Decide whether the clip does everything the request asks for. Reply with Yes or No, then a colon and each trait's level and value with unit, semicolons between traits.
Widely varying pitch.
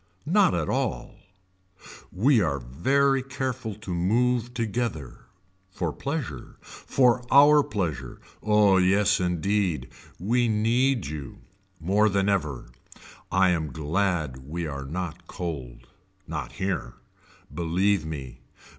Yes: wide, 7.2 semitones